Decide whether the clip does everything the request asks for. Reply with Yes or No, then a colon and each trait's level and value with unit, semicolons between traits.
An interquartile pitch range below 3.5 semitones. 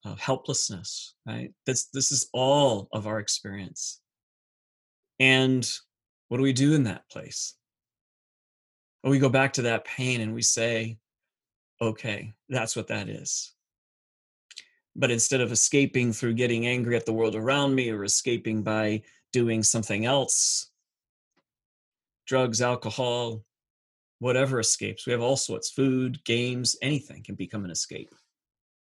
Yes: average, 3.0 semitones